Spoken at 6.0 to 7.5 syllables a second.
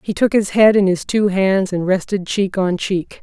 No: 4.5 syllables/s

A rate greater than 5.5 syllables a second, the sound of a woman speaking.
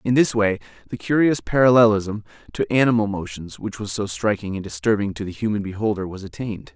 No: 6.0 syllables/s; male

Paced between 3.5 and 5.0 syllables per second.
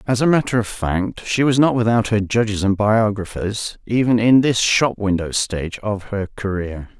Yes: 4.7 syllables/s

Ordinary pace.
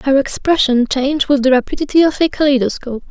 Yes: average, 175 wpm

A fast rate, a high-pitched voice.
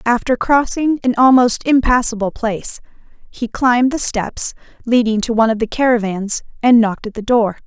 No: average, 165 wpm; high, 235 Hz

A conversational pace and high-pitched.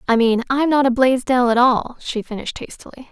No: fast, 210 wpm; very high, 250 Hz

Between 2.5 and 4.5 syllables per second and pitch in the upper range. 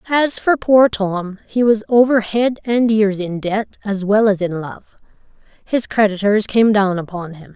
Yes: 4.2 syllables/s; high, 210 Hz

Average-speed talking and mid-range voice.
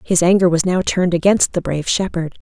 No: fast, 220 wpm; medium, 175 Hz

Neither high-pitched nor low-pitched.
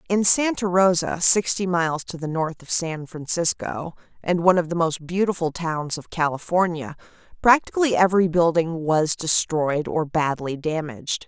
Yes: medium, 170 Hz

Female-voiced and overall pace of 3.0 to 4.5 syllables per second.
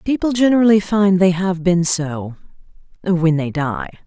Yes: female; 4.4 syllables/s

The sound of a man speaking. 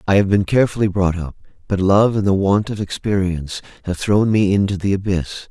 Yes: male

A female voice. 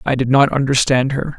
No: male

